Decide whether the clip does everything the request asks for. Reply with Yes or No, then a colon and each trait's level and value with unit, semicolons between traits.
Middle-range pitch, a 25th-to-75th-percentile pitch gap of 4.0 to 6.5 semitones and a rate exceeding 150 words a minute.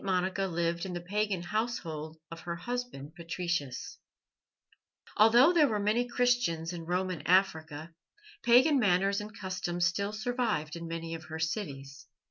No: medium, 180 Hz; average, 4.4 semitones; average, 140 wpm